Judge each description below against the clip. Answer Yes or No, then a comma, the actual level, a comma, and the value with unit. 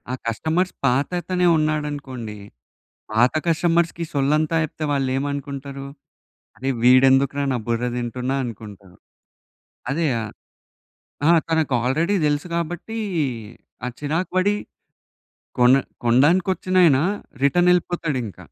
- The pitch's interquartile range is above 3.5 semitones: Yes, average, 4.6 semitones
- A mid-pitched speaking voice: Yes, medium, 145 Hz